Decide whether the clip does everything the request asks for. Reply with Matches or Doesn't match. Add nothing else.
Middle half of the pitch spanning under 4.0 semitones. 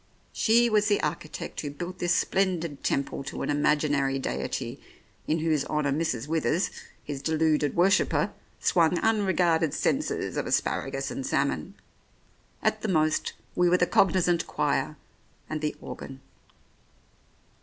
Matches